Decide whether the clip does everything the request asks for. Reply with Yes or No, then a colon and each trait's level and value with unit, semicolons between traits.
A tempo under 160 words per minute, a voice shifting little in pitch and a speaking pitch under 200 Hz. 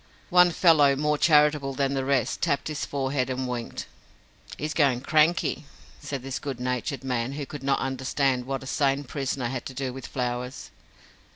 No: average, 175 wpm; narrow, 2.2 semitones; low, 135 Hz